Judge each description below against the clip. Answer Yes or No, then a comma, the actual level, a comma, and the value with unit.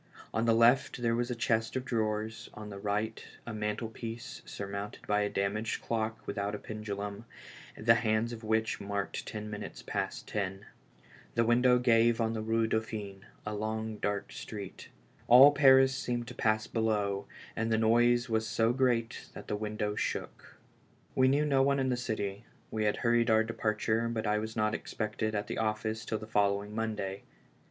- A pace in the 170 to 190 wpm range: Yes, average, 180 wpm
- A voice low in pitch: Yes, low, 110 Hz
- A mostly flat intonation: Yes, narrow, 1.7 semitones